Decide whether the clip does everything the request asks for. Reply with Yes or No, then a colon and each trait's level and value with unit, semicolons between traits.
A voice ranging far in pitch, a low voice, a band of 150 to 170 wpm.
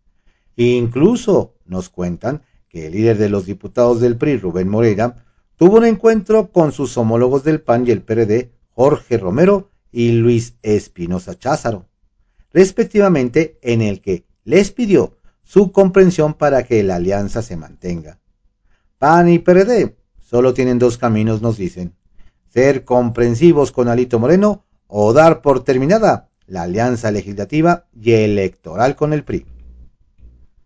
No: wide, 7.2 semitones; low, 120 Hz; average, 135 wpm